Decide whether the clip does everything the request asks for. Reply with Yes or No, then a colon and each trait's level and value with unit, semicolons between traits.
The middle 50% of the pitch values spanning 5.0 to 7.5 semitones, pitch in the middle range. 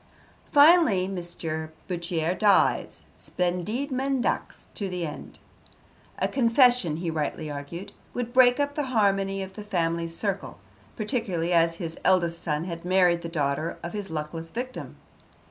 Yes: average, 5.3 semitones; medium, 180 Hz